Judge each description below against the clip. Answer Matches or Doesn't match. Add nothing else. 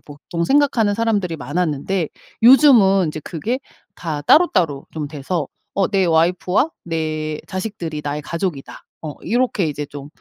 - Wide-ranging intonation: Doesn't match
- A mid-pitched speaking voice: Matches